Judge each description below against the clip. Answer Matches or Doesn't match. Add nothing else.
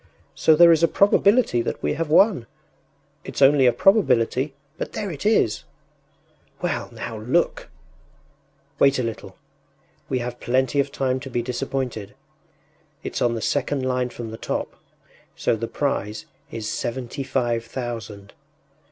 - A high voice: Doesn't match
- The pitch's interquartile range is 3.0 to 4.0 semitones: Matches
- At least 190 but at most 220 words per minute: Doesn't match